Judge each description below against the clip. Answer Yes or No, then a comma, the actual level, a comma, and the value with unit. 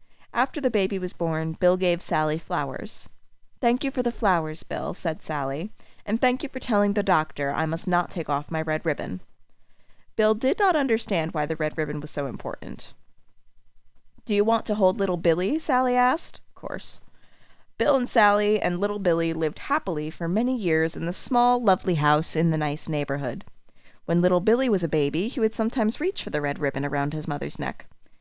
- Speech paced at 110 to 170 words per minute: No, average, 195 wpm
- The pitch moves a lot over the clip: Yes, wide, 5.9 semitones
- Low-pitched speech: No, medium, 180 Hz